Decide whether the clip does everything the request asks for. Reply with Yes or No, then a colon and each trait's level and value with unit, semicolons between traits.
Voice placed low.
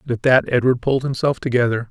Yes: low, 125 Hz